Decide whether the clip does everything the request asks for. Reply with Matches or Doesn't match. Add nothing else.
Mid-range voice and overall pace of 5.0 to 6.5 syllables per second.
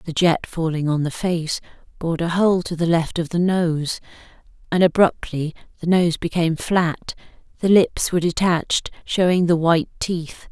Doesn't match